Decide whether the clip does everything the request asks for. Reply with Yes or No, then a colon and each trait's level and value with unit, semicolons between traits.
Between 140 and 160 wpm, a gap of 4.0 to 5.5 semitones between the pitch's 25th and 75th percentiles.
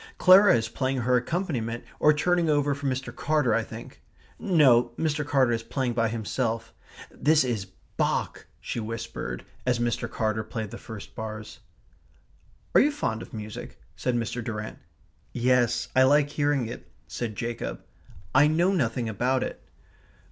Yes: average, 155 wpm; average, 4.3 semitones